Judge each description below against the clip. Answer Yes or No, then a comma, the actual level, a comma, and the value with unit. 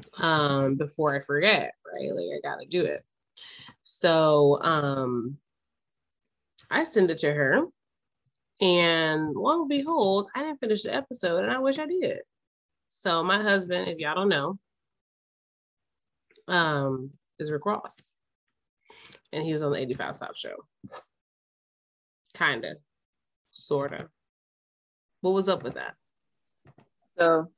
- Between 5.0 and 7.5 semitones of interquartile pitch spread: Yes, wide, 5.6 semitones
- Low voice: No, medium, 165 Hz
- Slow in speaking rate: Yes, slow, 130 wpm